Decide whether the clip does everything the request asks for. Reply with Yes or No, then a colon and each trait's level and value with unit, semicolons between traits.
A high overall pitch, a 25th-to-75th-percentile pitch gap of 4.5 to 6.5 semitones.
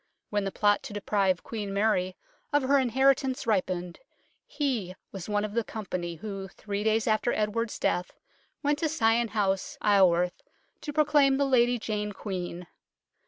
Yes: high, 215 Hz; average, 4.9 semitones